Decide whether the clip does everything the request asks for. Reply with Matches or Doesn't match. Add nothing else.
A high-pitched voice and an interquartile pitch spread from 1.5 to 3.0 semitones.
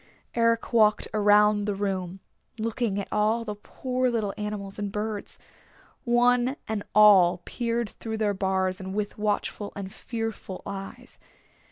Matches